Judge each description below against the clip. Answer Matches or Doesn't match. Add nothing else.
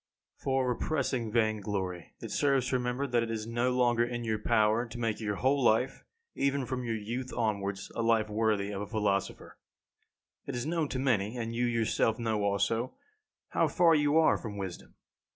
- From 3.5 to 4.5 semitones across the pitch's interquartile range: Doesn't match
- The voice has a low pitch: Matches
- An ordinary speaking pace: Matches